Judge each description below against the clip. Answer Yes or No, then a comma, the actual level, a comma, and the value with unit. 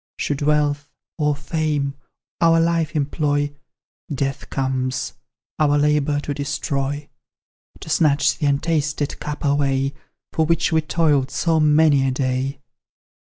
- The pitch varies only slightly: Yes, narrow, 1.6 semitones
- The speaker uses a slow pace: Yes, slow, 120 wpm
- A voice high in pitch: No, medium, 145 Hz